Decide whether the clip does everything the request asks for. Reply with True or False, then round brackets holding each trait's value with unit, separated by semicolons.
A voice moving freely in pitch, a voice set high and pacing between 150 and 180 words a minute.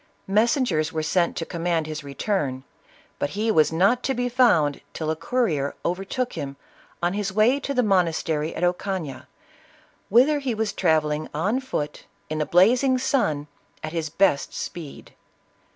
False (7.0 semitones; 175 Hz; 155 wpm)